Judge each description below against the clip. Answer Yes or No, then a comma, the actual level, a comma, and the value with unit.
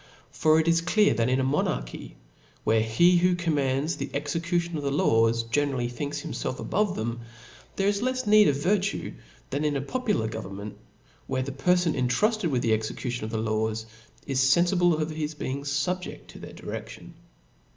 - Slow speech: No, average, 180 wpm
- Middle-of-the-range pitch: Yes, medium, 145 Hz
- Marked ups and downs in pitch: Yes, wide, 6.4 semitones